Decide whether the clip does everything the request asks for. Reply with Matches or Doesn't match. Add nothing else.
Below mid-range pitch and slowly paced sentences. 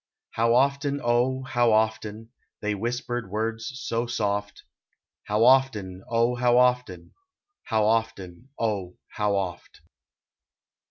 Matches